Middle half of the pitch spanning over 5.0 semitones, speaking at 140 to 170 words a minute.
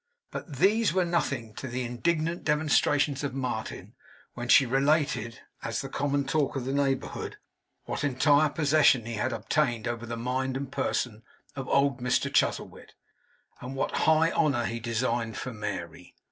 No: average, 3.5 semitones; average, 160 wpm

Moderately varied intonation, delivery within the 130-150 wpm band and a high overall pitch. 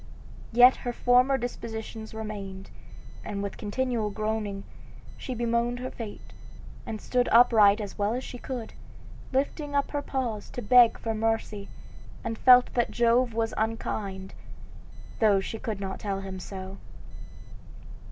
Yes: average, 3.1 semitones; average, 140 wpm; high, 225 Hz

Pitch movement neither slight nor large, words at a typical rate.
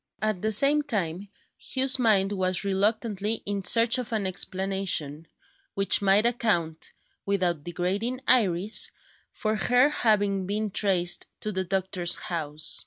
No: average, 3.1 semitones; slow, 130 wpm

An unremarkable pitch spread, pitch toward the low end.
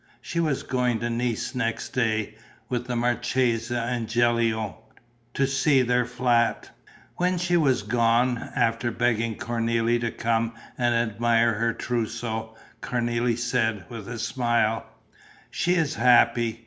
No: narrow, 1.3 semitones; low, 120 Hz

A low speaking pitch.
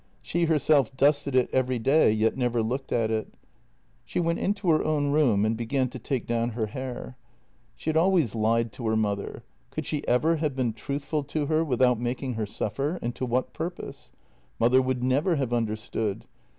Yes: low, 130 Hz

